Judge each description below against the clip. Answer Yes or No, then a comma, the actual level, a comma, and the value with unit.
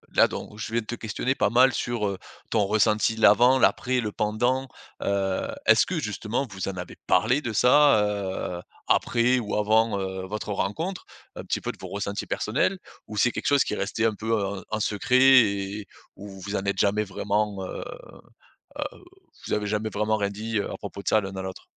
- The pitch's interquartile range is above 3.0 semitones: No, average, 2.7 semitones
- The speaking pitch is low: Yes, low, 105 Hz